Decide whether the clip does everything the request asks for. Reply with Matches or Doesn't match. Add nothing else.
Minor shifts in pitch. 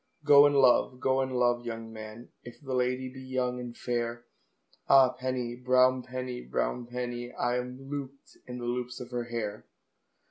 Matches